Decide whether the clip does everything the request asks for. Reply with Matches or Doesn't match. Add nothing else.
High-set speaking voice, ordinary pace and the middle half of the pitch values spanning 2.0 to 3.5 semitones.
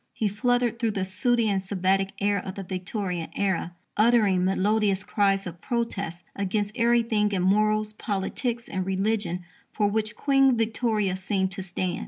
Matches